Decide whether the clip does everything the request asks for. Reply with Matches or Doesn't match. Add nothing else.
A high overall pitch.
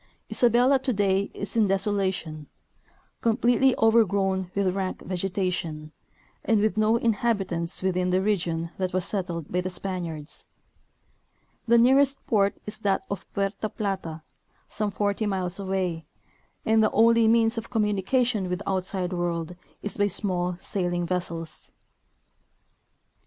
Matches